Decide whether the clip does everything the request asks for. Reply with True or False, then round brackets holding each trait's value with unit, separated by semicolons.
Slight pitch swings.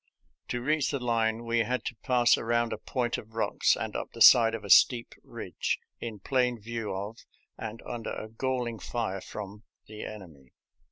True (2.0 semitones)